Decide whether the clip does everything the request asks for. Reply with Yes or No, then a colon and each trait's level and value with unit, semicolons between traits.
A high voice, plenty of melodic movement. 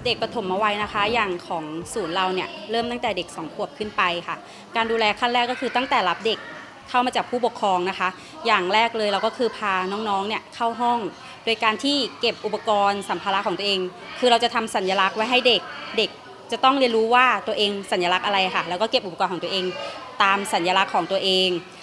No: high, 215 Hz; average, 3.8 semitones